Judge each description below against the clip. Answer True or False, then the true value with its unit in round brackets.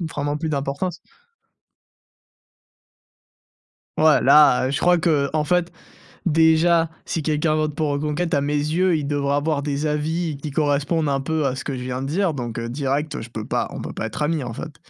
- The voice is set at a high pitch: False (150 Hz)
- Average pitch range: False (2.3 semitones)